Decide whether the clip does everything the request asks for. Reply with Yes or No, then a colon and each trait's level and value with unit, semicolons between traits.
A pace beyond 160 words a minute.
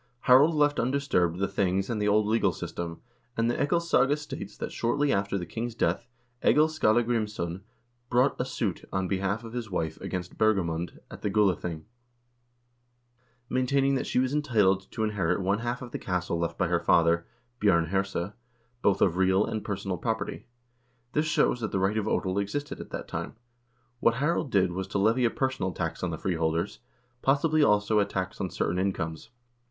Yes: average, 180 wpm